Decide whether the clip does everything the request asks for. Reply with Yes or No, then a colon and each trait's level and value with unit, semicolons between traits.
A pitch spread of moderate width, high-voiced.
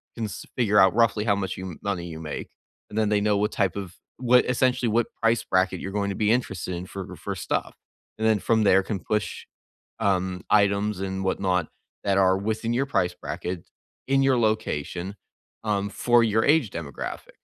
No: average, 3.0 semitones; low, 100 Hz